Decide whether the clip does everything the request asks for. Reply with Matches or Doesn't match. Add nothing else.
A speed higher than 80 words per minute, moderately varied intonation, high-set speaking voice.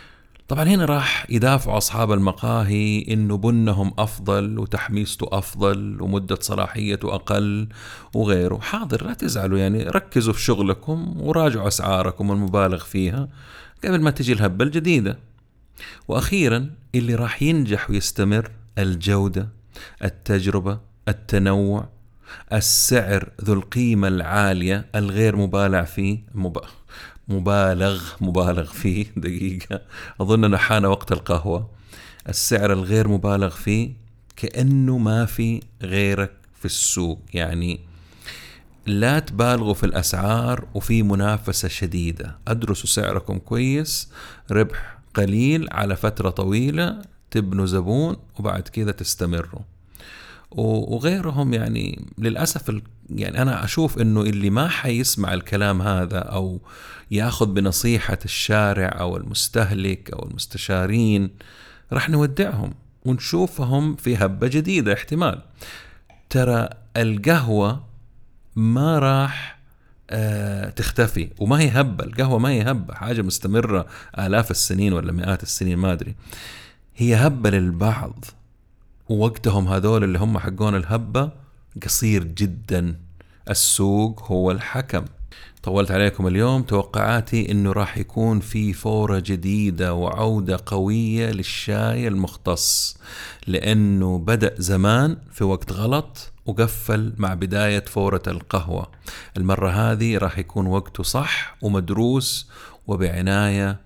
Doesn't match